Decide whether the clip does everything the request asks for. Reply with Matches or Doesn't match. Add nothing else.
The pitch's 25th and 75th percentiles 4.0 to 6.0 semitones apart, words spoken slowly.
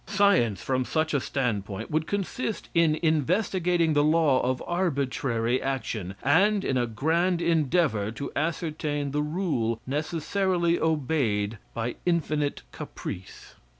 Matches